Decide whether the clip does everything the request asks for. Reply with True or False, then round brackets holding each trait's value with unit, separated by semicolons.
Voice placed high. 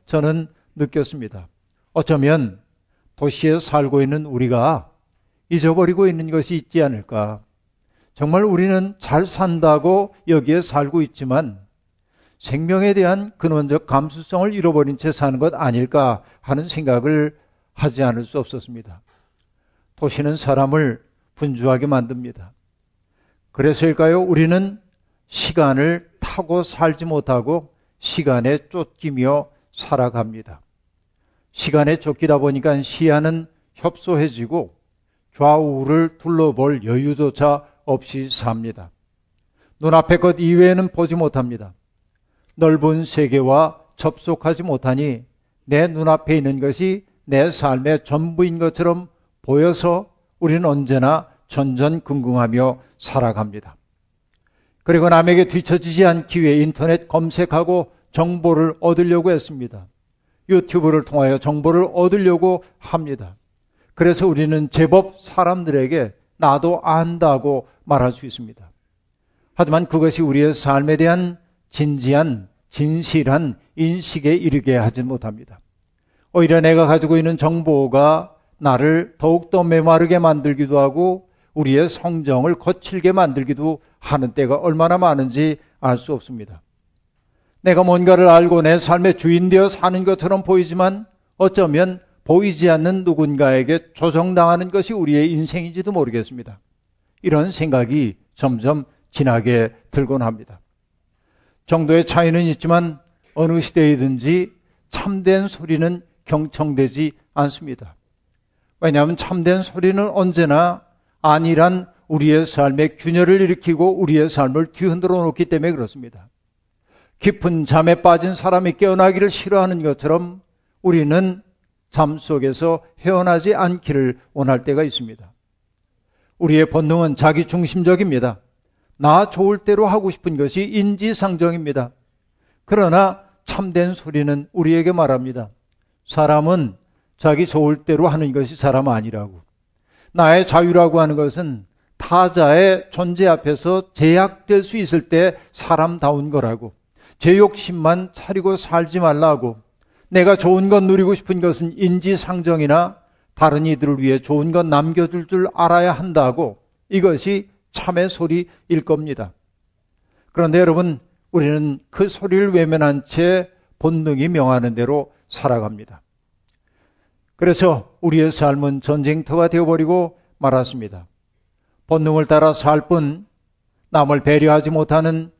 False (155 Hz)